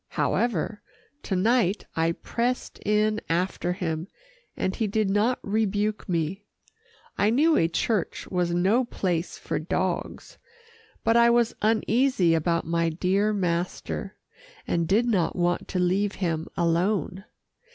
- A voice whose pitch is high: Yes, high, 195 Hz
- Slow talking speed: Yes, slow, 130 wpm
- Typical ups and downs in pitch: Yes, average, 3.9 semitones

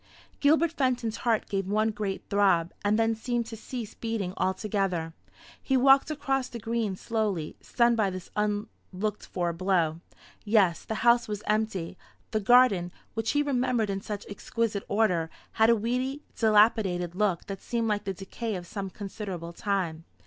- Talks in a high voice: Yes, high, 210 Hz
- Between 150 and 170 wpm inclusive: Yes, average, 160 wpm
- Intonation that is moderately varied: Yes, average, 3.3 semitones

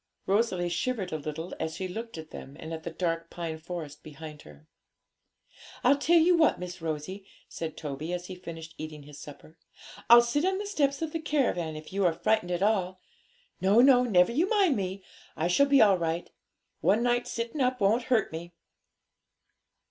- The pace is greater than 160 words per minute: Yes, average, 190 wpm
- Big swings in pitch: Yes, wide, 7.0 semitones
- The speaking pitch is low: No, medium, 180 Hz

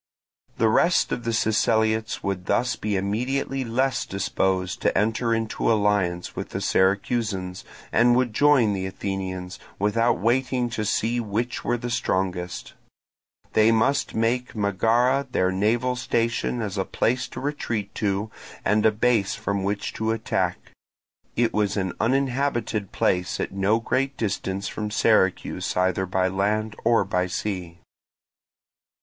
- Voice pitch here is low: Yes, low, 110 Hz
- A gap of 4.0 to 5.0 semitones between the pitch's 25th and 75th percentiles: No, average, 3.6 semitones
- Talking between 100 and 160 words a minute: Yes, average, 140 wpm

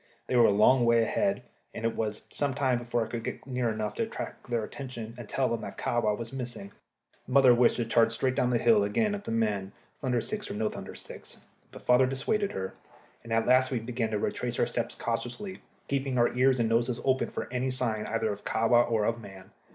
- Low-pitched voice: Yes, low, 120 Hz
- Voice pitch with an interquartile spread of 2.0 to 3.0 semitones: Yes, narrow, 2.4 semitones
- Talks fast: Yes, fast, 230 wpm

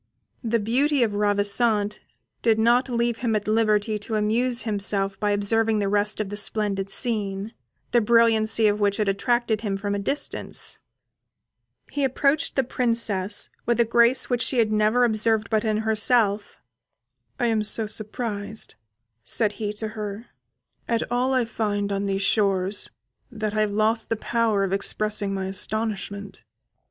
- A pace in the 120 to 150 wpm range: No, average, 160 wpm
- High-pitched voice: Yes, high, 215 Hz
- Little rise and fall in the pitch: Yes, narrow, 2.2 semitones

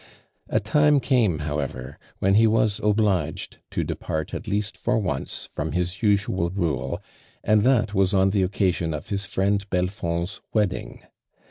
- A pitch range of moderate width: Yes, average, 3.6 semitones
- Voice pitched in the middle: No, very low, 95 Hz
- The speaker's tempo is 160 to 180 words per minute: No, average, 150 wpm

